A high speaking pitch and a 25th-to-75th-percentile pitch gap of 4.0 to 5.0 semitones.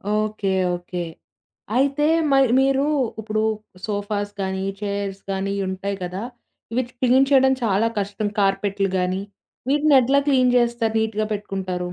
Yes: high, 210 Hz; average, 4.4 semitones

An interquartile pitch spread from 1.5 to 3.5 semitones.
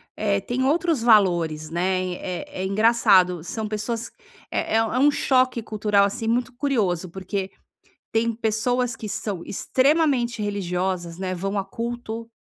No: average, 4.1 semitones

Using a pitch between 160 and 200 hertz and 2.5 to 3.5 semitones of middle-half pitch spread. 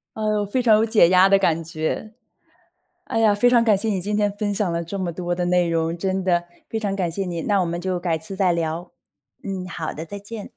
Yes: high, 190 Hz; average, 3.2 semitones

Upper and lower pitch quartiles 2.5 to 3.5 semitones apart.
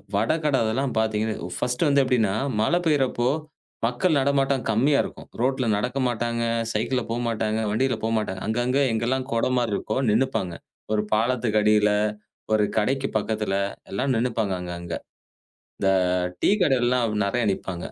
Yes: average, 3.2 semitones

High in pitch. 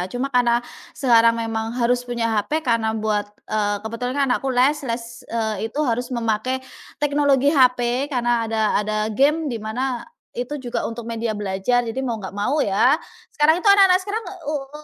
Yes: high, 240 Hz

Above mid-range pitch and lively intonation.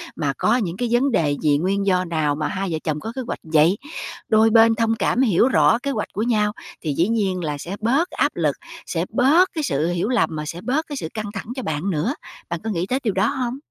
Yes: high, 200 Hz; wide, 6.3 semitones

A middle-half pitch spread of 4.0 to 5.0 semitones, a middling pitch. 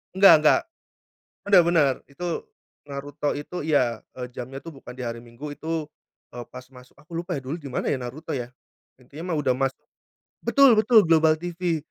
Yes: average, 4.6 semitones; medium, 145 Hz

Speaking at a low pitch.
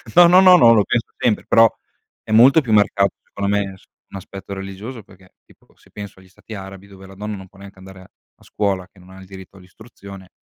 Yes: low, 100 Hz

